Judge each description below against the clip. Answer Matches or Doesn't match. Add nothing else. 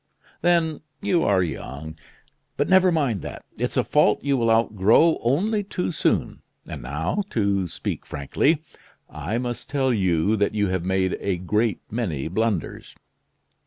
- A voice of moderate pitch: Doesn't match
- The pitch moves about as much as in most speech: Doesn't match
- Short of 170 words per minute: Matches